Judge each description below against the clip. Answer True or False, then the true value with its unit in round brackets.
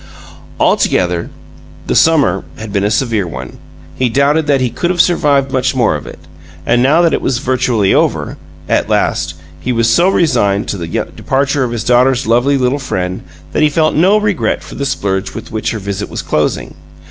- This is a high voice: False (125 Hz)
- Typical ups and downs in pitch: False (5.8 semitones)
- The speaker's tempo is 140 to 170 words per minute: False (195 wpm)